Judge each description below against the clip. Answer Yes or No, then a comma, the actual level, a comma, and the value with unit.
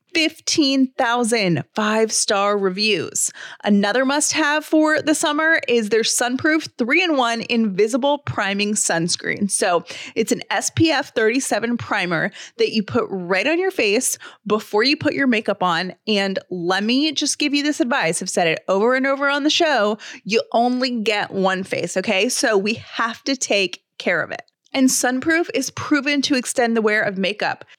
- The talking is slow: No, average, 170 wpm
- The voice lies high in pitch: Yes, high, 235 Hz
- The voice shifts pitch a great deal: Yes, wide, 6.0 semitones